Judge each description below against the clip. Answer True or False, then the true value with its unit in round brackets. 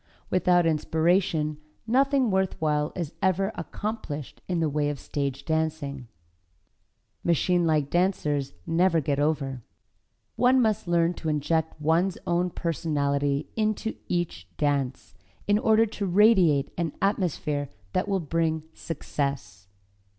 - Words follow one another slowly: True (120 wpm)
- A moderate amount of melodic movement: True (4.2 semitones)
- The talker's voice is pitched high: False (165 Hz)